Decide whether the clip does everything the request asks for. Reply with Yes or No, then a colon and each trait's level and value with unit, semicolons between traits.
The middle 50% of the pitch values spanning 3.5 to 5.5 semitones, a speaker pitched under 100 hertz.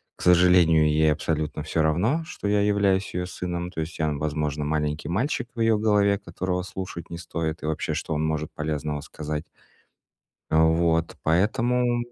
Yes: average, 4.1 semitones; very low, 85 Hz